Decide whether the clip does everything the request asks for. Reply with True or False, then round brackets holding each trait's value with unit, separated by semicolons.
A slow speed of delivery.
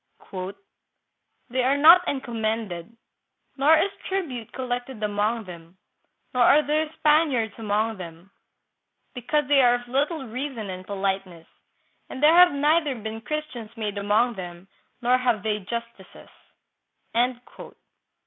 True (125 wpm)